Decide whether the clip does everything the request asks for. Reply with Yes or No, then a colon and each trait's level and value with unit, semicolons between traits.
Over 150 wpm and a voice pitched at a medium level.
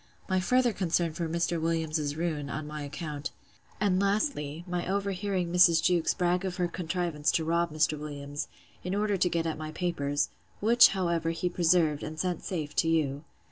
Yes: average, 180 wpm; medium, 170 Hz